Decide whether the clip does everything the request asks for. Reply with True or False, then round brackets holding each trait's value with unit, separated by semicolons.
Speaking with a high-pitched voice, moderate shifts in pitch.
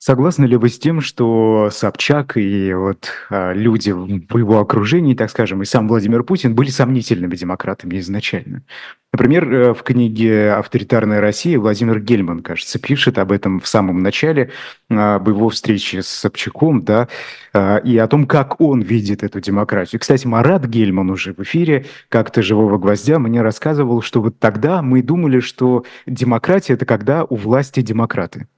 False (115 Hz; 4.0 semitones)